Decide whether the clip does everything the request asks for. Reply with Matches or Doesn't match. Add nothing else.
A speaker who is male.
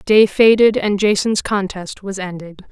Doesn't match